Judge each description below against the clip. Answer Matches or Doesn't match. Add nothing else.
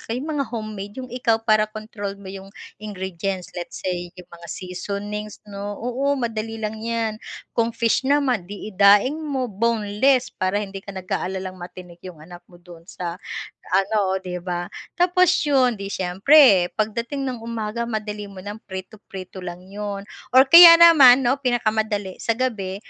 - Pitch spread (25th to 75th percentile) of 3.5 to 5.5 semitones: Matches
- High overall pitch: Matches